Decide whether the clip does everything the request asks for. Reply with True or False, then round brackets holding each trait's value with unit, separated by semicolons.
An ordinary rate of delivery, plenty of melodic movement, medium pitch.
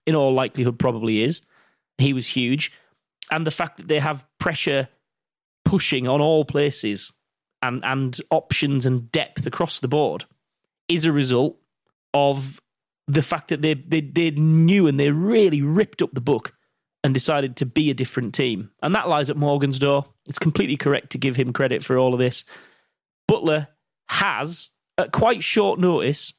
False (170 wpm; 3.0 semitones; 145 Hz)